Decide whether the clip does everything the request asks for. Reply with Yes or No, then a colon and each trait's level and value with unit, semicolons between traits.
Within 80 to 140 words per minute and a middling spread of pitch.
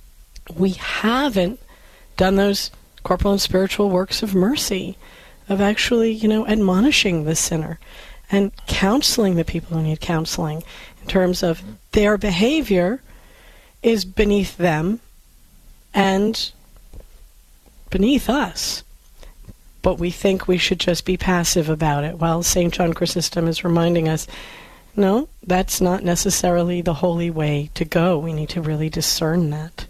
Yes: slow, 135 wpm; average, 3.4 semitones